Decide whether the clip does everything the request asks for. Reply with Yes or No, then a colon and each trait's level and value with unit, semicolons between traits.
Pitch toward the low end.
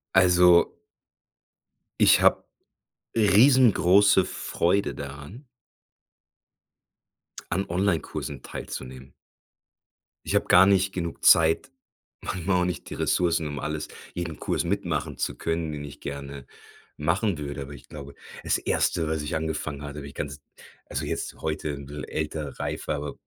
Yes: very low, 80 Hz